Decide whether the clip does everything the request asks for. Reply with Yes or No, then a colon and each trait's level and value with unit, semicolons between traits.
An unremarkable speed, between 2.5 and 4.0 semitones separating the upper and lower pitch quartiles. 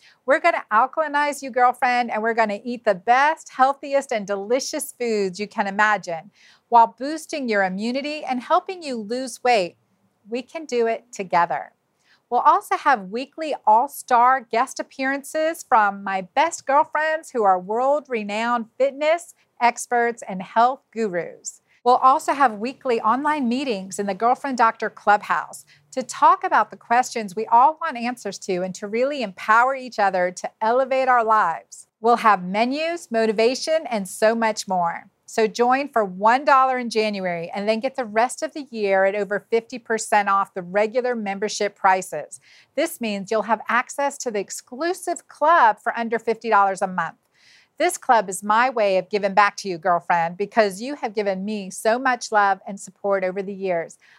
No: average, 170 wpm; average, 4.6 semitones